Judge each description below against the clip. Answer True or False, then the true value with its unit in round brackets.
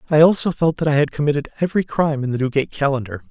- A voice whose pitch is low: False (145 Hz)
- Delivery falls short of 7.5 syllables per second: False (7.7 syllables/s)